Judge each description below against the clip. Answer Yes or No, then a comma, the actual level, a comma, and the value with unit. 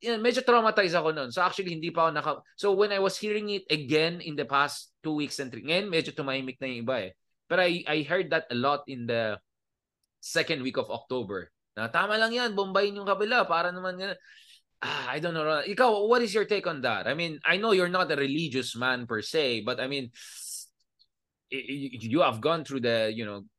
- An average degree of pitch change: No, wide, 7.0 semitones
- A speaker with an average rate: Yes, average, 175 wpm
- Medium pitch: Yes, medium, 155 Hz